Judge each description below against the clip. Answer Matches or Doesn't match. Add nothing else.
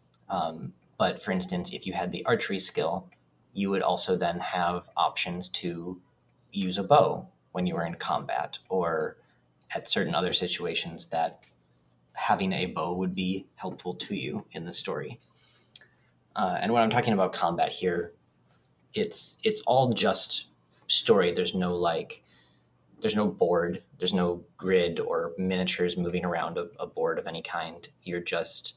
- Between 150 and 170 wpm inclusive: Matches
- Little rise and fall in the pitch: Matches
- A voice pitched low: Matches